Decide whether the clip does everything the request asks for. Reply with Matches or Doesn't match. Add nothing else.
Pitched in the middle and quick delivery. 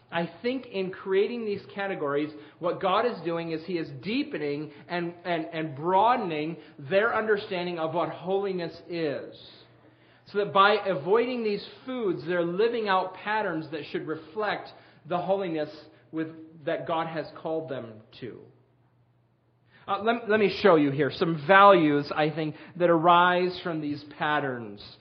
Doesn't match